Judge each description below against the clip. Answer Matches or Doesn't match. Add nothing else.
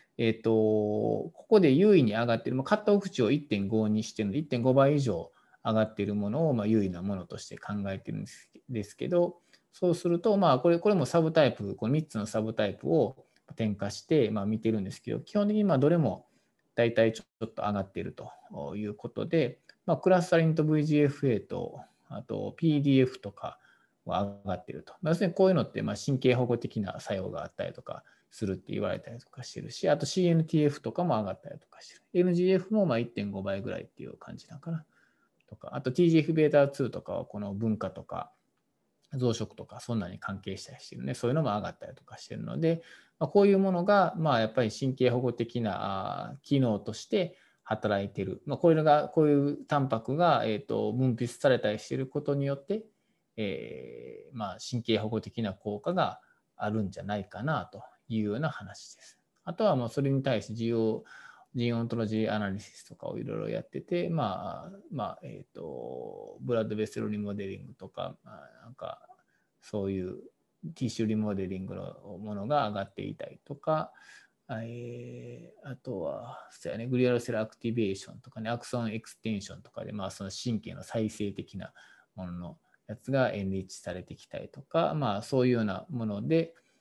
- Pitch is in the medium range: Doesn't match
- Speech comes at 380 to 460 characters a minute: Matches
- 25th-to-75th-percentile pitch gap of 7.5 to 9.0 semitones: Doesn't match